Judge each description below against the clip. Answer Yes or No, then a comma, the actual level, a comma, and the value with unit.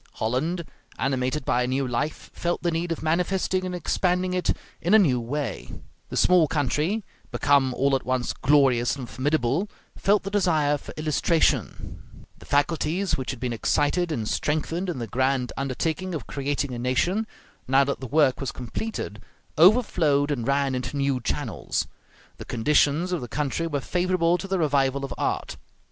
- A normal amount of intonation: Yes, average, 4.9 semitones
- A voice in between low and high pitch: Yes, medium, 145 Hz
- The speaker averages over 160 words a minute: Yes, average, 170 wpm